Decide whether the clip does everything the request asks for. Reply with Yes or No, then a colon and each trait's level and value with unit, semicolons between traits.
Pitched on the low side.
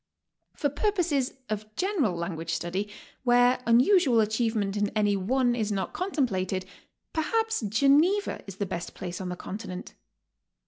No: high, 220 Hz